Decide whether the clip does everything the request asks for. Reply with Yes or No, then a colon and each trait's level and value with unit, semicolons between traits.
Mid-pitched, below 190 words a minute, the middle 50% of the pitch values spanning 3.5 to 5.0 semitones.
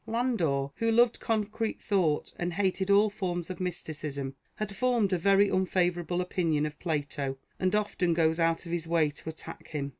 Yes: medium, 175 Hz; average, 175 wpm; average, 4.1 semitones